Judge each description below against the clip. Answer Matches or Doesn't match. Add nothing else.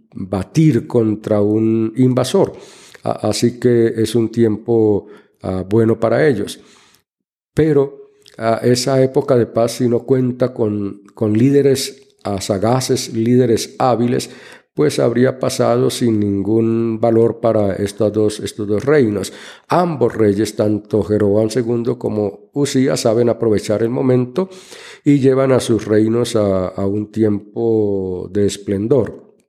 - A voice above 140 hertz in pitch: Doesn't match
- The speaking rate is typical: Doesn't match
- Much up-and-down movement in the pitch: Doesn't match